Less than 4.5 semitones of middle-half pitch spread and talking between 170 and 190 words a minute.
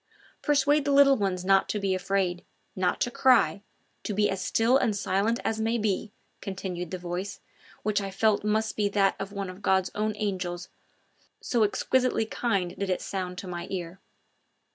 Yes: average, 2.9 semitones; average, 180 wpm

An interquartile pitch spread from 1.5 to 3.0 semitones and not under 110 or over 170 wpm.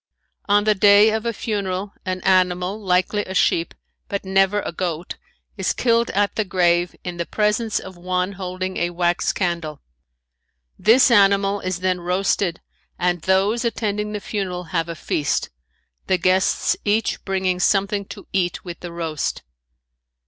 Yes: narrow, 2.4 semitones; average, 155 wpm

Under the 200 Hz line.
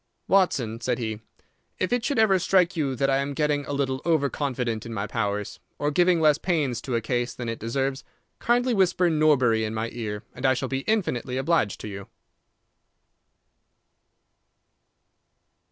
Yes: low, 135 Hz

